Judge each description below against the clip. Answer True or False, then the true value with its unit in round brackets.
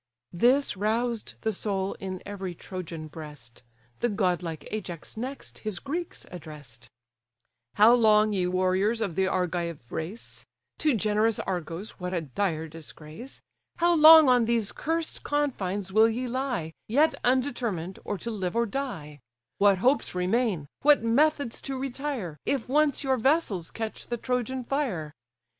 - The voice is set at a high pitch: True (215 Hz)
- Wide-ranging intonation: True (6.0 semitones)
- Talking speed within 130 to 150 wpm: True (145 wpm)